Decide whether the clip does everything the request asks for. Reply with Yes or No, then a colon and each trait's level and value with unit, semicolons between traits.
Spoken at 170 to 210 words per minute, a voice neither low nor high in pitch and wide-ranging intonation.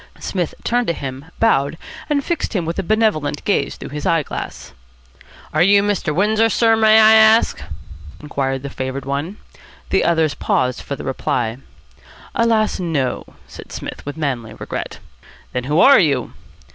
No: average, 160 wpm; medium, 165 Hz; wide, 7.7 semitones